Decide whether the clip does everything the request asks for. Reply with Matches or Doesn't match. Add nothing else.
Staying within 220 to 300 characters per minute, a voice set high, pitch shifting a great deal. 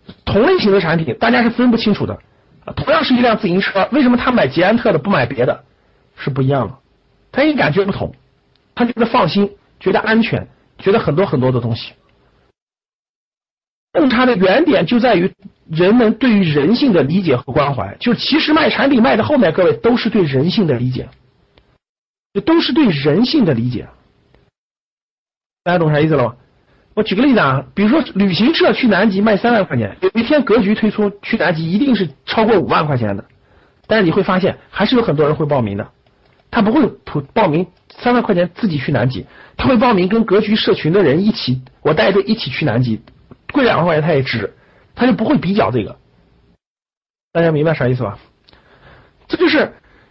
Matches